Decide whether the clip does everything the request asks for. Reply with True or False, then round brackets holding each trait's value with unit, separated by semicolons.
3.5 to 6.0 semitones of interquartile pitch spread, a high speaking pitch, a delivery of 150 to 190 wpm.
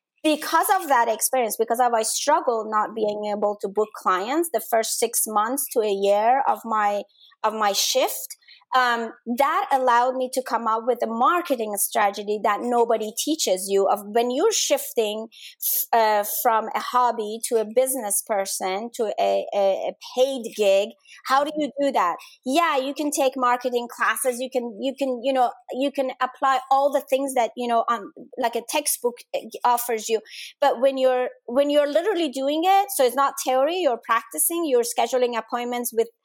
True (3.8 semitones; 245 Hz; 180 wpm)